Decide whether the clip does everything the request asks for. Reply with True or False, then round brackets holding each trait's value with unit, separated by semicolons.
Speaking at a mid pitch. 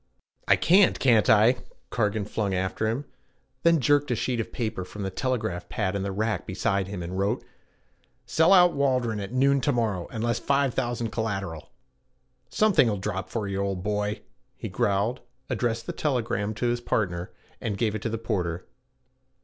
False (110 Hz)